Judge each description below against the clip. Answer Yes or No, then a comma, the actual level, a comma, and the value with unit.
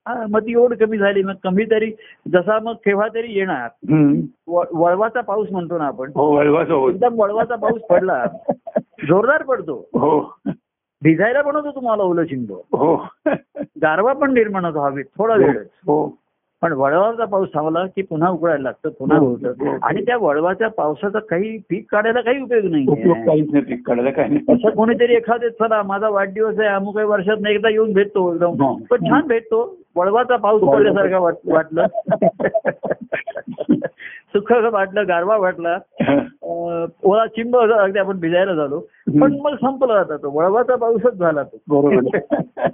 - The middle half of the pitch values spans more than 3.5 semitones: Yes, average, 5.1 semitones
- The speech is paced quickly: Yes, fast, 135 wpm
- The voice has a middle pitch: No, high, 205 Hz